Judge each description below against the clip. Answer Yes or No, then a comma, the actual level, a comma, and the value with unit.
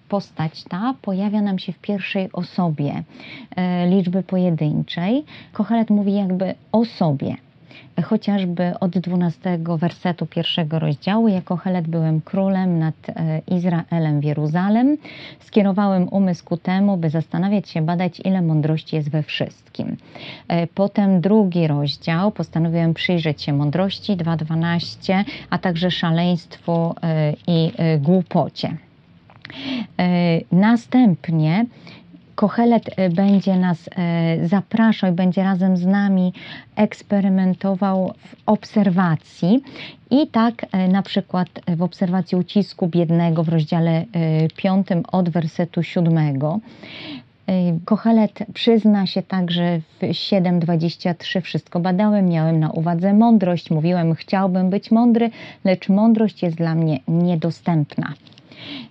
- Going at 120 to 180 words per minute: No, slow, 110 wpm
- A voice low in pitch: No, medium, 180 Hz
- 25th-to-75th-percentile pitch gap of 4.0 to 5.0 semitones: No, average, 3.1 semitones